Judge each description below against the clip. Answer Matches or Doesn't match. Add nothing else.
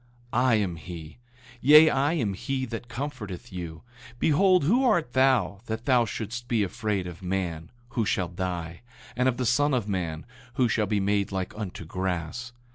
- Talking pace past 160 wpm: Matches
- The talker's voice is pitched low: Matches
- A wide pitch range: Matches